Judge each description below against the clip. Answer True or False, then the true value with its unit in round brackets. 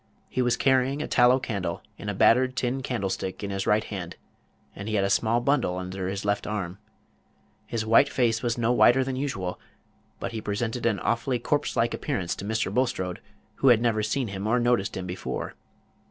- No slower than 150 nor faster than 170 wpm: False (195 wpm)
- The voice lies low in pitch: True (115 Hz)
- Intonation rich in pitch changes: False (4.0 semitones)